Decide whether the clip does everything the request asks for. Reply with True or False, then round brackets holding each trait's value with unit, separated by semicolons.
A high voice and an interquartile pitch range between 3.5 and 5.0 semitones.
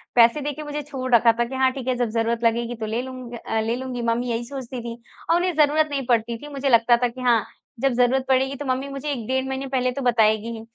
False (250 Hz; 2.4 semitones)